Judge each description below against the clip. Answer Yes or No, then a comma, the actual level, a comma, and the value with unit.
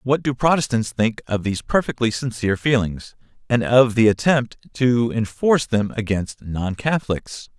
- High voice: No, low, 115 Hz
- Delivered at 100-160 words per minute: Yes, average, 150 wpm